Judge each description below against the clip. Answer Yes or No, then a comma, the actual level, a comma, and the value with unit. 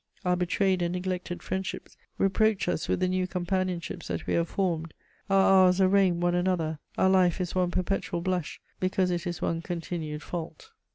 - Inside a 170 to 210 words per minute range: Yes, average, 175 wpm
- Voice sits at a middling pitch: Yes, medium, 180 Hz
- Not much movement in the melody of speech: Yes, narrow, 1.5 semitones